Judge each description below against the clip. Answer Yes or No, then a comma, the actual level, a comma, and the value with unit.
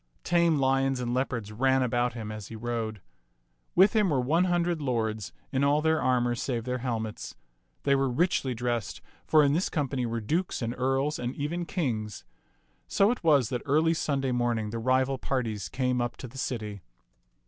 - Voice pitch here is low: Yes, low, 130 Hz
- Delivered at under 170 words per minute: No, average, 180 wpm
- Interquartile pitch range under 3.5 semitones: No, average, 3.8 semitones